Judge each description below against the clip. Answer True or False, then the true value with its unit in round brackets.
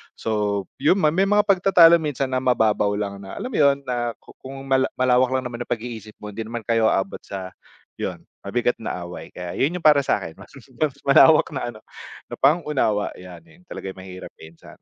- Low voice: True (125 Hz)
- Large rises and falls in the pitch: True (5.8 semitones)